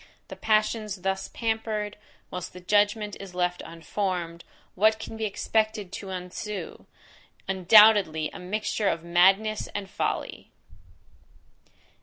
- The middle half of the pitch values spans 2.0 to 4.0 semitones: Yes, average, 3.0 semitones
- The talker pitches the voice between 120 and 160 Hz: No, high, 200 Hz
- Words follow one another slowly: Yes, slow, 115 wpm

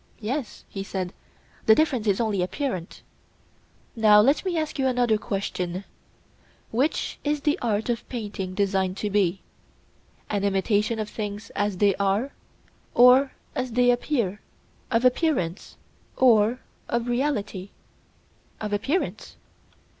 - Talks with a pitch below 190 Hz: No, high, 215 Hz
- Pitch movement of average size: Yes, average, 4.0 semitones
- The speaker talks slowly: Yes, slow, 120 wpm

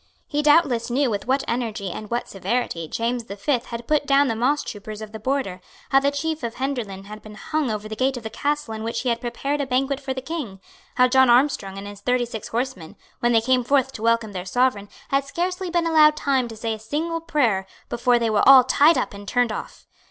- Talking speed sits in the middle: No, fast, 235 wpm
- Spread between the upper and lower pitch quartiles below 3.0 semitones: No, average, 4.3 semitones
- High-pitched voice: Yes, high, 245 Hz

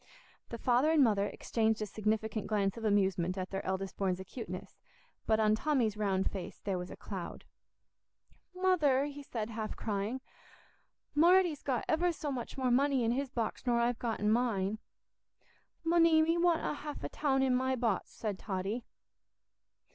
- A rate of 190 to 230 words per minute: No, average, 165 wpm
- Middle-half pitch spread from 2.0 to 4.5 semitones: No, average, 5.3 semitones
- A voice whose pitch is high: Yes, high, 230 Hz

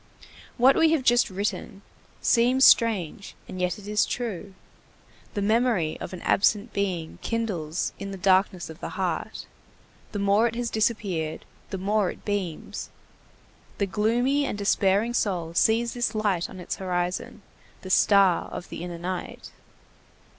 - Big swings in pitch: No, average, 3.9 semitones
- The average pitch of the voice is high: Yes, high, 200 Hz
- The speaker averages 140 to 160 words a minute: Yes, average, 150 wpm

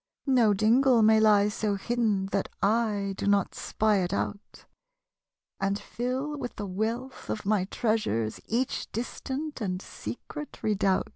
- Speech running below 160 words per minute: Yes, average, 140 wpm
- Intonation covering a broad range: No, average, 3.4 semitones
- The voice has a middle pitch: No, high, 215 Hz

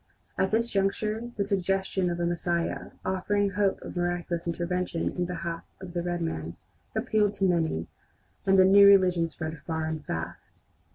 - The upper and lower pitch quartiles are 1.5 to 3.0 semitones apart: Yes, narrow, 2.4 semitones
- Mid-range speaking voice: Yes, medium, 180 Hz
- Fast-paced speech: No, average, 165 wpm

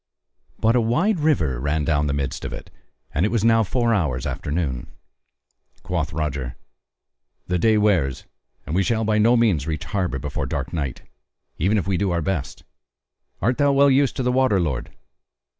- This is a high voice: No, very low, 95 Hz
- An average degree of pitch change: No, wide, 7.6 semitones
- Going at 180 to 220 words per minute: Yes, average, 185 wpm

